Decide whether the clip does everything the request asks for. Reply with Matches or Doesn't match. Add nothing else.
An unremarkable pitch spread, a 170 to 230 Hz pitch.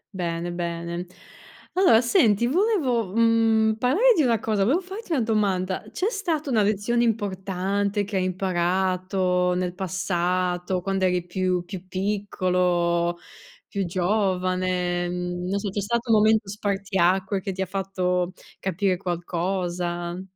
Matches